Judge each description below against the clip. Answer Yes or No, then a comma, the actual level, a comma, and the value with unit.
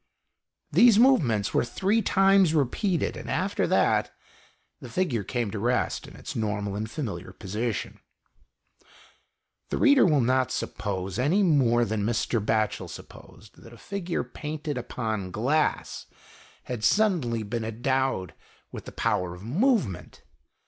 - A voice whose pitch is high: No, low, 120 Hz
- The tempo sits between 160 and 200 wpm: No, slow, 135 wpm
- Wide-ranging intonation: Yes, wide, 7.1 semitones